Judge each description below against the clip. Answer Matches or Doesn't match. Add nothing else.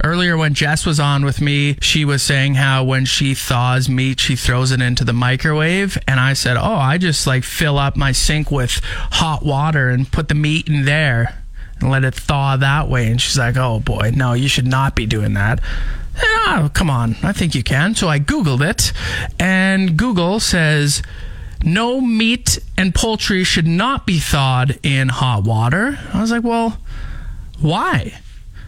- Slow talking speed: Doesn't match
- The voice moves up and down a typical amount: Matches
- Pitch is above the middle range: Doesn't match